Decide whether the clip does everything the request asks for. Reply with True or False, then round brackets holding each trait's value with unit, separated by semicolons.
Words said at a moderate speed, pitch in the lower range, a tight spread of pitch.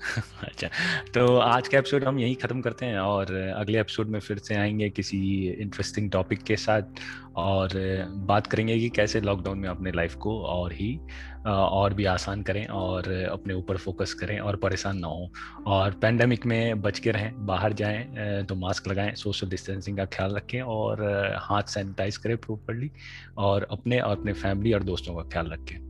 True (180 wpm; 100 Hz; 2.3 semitones)